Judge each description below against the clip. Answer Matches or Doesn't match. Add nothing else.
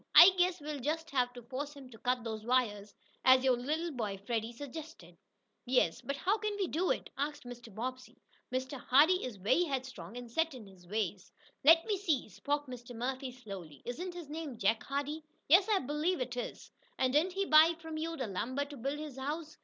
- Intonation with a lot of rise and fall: Doesn't match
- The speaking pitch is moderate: Doesn't match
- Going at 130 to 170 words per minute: Doesn't match